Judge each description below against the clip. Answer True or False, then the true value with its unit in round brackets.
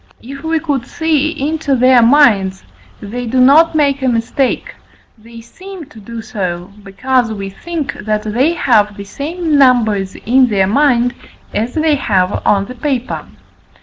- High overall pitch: True (245 Hz)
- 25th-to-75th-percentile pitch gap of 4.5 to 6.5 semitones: True (5.3 semitones)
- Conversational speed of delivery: True (155 wpm)